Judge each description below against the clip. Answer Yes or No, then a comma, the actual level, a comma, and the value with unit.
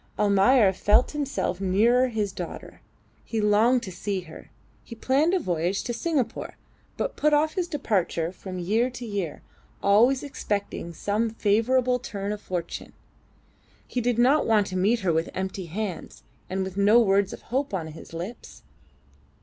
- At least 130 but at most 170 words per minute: Yes, average, 160 wpm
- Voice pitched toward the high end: Yes, high, 210 Hz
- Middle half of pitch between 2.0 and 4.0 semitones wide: No, average, 4.6 semitones